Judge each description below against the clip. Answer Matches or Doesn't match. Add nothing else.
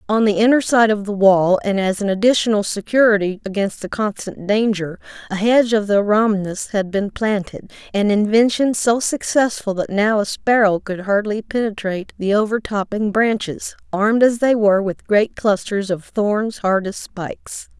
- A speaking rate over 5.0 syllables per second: Doesn't match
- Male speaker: Doesn't match